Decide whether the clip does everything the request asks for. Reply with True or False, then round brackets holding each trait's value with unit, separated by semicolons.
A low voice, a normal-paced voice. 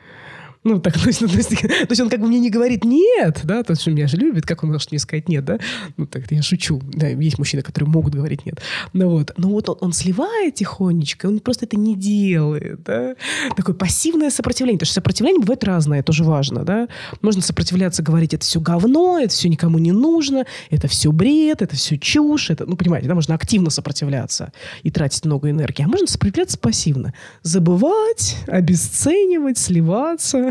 False (180 Hz; 195 wpm)